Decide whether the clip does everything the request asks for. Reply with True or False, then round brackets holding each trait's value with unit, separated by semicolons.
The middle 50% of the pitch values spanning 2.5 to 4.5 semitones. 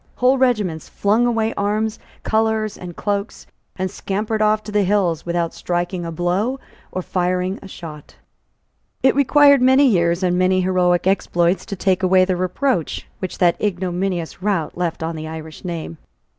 True (3.5 semitones)